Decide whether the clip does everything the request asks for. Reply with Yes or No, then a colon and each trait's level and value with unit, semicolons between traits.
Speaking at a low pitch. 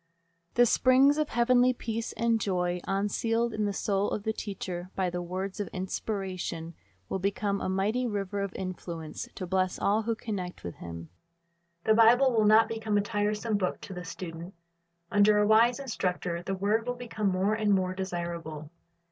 No: high, 200 Hz